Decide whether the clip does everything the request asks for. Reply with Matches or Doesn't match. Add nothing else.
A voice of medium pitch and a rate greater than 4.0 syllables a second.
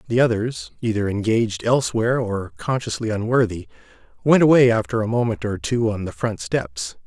Doesn't match